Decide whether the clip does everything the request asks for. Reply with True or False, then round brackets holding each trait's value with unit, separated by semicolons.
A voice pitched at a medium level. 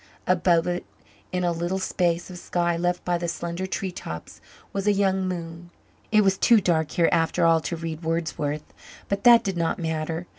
True (175 Hz)